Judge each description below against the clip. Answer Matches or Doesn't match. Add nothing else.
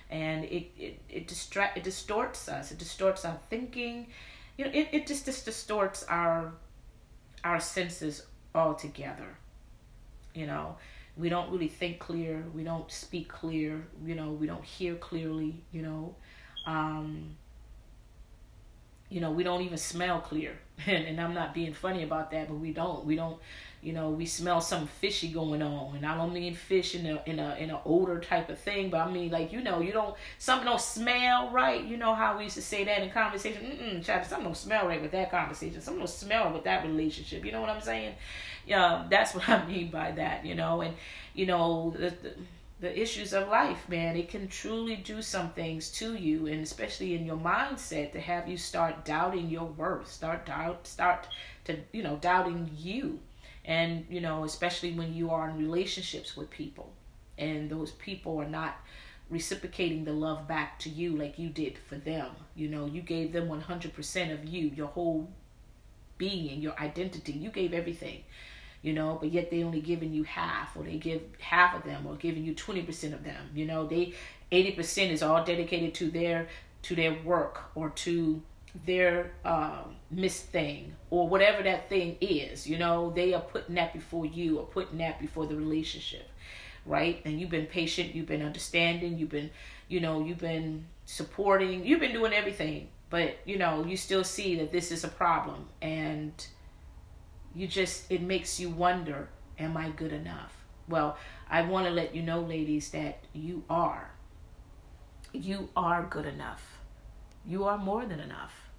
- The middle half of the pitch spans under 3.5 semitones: Matches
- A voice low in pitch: Doesn't match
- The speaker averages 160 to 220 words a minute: Matches